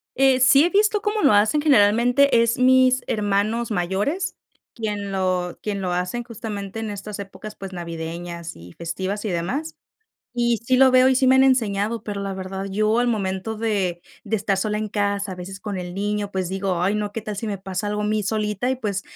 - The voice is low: No, high, 210 Hz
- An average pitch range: Yes, average, 3.7 semitones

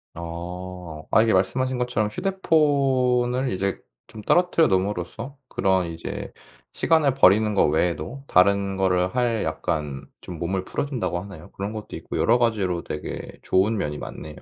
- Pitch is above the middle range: No, low, 100 Hz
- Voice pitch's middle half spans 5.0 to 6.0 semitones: Yes, wide, 5.6 semitones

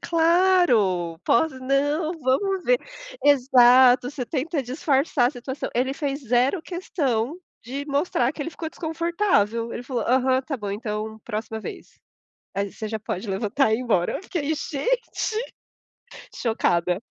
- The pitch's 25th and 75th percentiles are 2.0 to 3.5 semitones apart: No, wide, 5.6 semitones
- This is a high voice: Yes, very high, 260 Hz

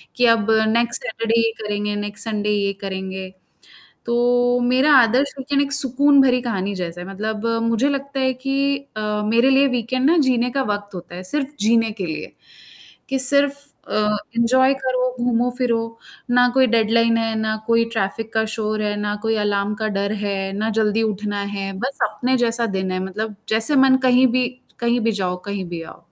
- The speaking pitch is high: Yes, high, 230 Hz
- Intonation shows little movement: No, average, 3.6 semitones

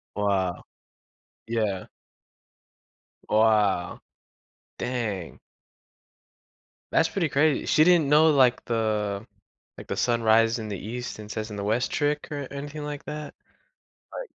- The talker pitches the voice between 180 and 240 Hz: No, low, 115 Hz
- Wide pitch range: Yes, wide, 5.7 semitones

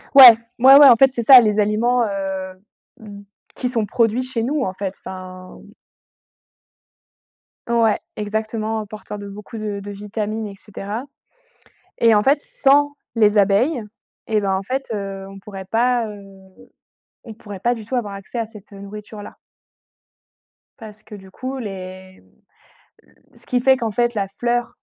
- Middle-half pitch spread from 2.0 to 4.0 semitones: Yes, average, 3.2 semitones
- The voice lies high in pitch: Yes, high, 215 Hz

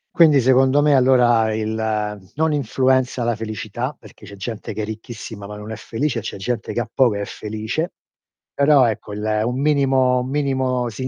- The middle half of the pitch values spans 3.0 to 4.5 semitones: Yes, average, 3.5 semitones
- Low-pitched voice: Yes, low, 125 Hz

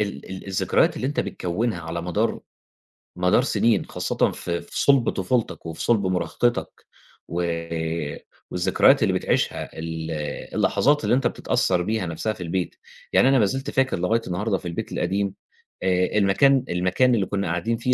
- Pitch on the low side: Yes, very low, 95 Hz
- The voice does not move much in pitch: No, average, 5.0 semitones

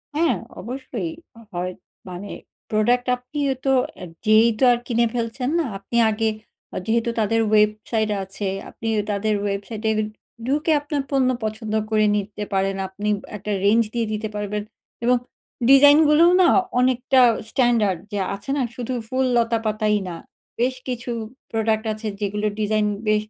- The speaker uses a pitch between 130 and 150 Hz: No, high, 225 Hz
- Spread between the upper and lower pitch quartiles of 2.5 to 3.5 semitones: Yes, average, 3.0 semitones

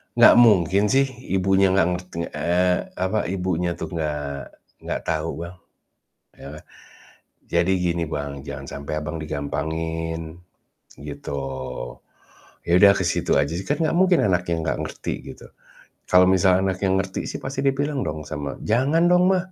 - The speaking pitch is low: Yes, very low, 90 Hz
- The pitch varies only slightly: No, average, 3.9 semitones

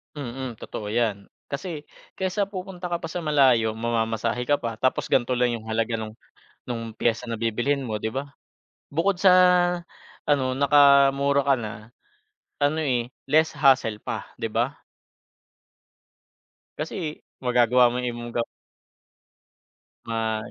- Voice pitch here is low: Yes, low, 125 Hz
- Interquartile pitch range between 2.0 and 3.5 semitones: No, average, 4.0 semitones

